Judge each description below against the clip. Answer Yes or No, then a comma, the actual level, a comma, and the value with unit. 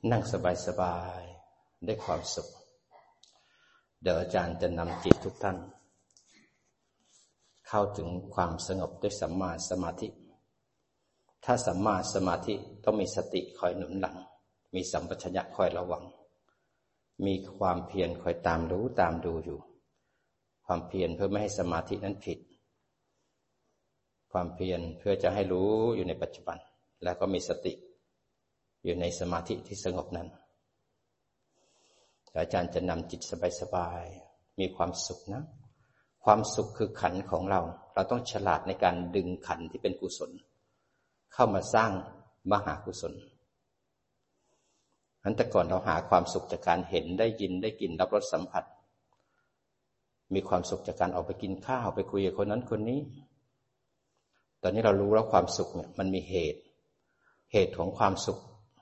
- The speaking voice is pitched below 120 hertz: Yes, very low, 95 Hz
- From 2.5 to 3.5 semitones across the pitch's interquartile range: Yes, average, 3.1 semitones